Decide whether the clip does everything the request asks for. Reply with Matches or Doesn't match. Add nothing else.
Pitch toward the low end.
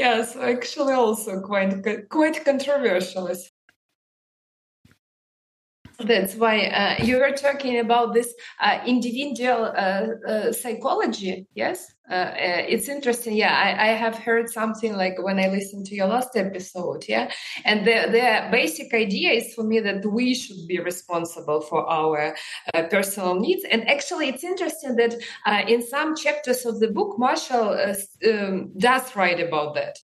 Doesn't match